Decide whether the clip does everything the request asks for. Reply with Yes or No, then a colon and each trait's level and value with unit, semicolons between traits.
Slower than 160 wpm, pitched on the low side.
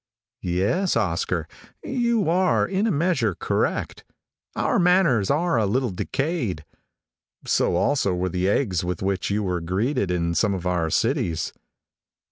Yes: average, 140 wpm; low, 105 Hz